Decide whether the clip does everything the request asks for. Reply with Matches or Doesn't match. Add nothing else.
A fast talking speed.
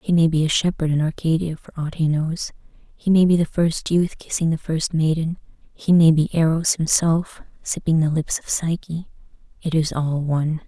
Doesn't match